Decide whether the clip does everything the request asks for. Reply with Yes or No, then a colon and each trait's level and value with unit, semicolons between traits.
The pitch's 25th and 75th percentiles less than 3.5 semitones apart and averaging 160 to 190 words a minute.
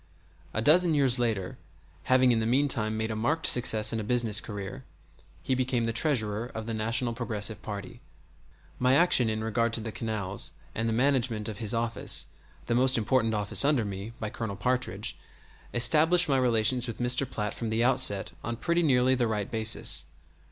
Yes: average, 2.8 semitones; average, 180 wpm